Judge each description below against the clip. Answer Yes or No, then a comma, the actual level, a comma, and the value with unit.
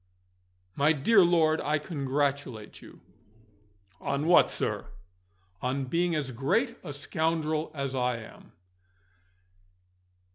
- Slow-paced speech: Yes, slow, 105 wpm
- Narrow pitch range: No, average, 3.2 semitones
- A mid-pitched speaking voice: Yes, medium, 145 Hz